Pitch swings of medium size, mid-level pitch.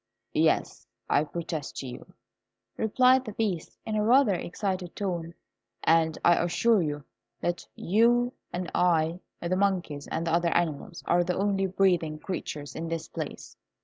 Yes: average, 3.4 semitones; medium, 175 Hz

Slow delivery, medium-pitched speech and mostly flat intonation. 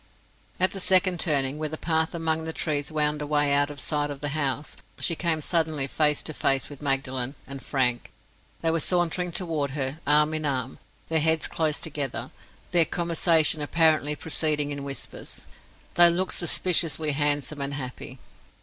No: average, 170 wpm; medium, 150 Hz; narrow, 2.3 semitones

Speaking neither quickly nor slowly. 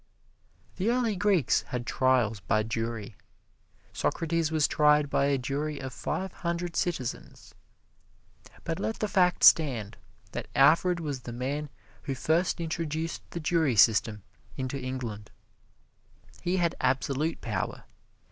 No: slow, 130 wpm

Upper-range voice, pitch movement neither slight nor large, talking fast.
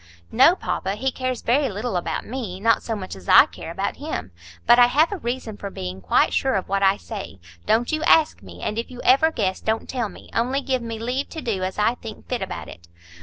Yes: high, 230 Hz; average, 4.6 semitones; fast, 235 wpm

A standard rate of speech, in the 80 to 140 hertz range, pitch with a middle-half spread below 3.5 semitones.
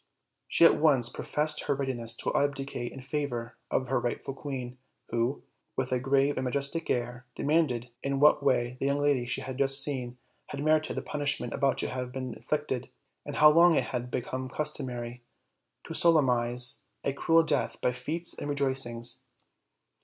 Yes: average, 175 wpm; low, 135 Hz; average, 2.8 semitones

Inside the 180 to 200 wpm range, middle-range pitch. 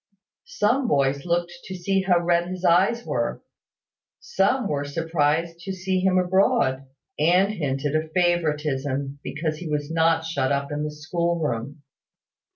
No: average, 150 wpm; medium, 165 Hz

